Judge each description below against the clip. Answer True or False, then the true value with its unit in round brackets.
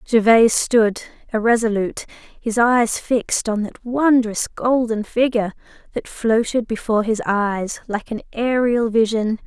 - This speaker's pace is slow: True (125 wpm)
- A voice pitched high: True (225 Hz)